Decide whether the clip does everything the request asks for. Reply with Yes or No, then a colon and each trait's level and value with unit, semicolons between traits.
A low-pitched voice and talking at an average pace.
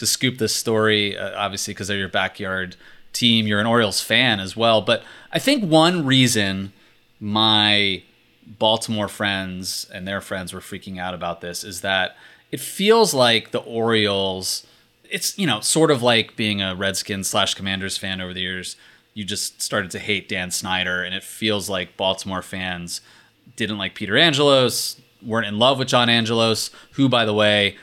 Yes: low, 105 Hz; average, 175 wpm